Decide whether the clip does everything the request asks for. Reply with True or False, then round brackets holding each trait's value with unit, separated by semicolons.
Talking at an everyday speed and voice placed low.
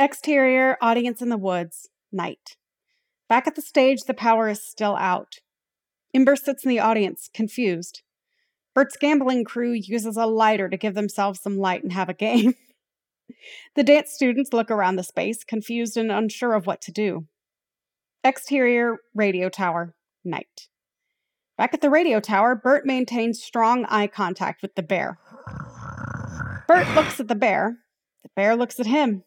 False (160 wpm; 235 Hz)